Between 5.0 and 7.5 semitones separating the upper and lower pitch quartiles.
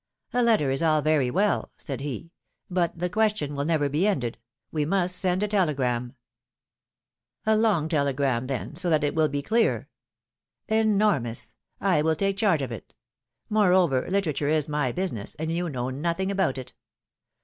Yes: wide, 5.5 semitones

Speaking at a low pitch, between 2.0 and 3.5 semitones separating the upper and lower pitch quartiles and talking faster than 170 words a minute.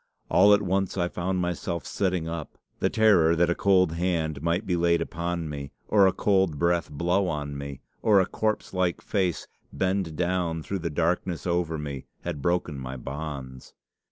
Yes: very low, 85 Hz; average, 2.9 semitones; average, 180 wpm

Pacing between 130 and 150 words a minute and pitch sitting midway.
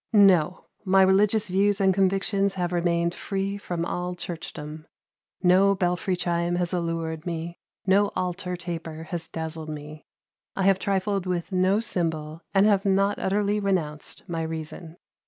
Yes: average, 145 wpm; medium, 180 Hz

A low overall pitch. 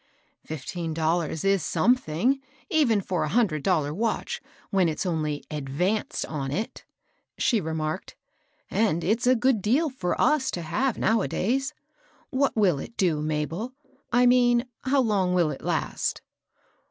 No: high, 190 Hz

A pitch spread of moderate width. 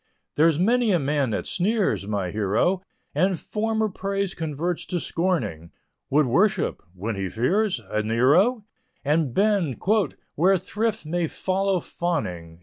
No: wide, 8.5 semitones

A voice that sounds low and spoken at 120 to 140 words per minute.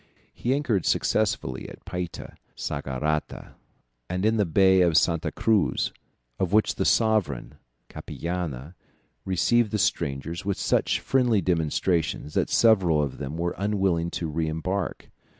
Yes: very low, 90 Hz; slow, 135 wpm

